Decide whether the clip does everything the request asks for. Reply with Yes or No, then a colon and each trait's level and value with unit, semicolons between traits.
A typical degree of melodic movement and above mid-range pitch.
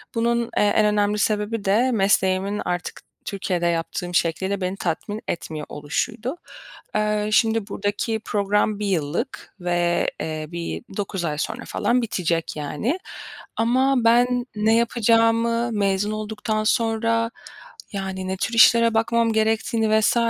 Yes: average, 3.3 semitones; high, 210 Hz